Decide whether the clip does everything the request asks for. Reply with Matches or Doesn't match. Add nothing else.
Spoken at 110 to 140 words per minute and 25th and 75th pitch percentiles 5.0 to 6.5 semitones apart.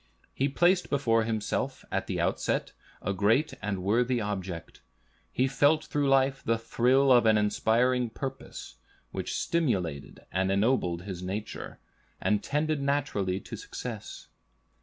Matches